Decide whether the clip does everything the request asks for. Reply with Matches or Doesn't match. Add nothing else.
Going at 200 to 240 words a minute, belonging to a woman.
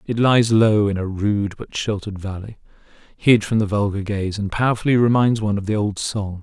Doesn't match